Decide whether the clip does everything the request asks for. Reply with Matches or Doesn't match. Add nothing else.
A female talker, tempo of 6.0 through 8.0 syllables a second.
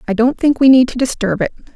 Matches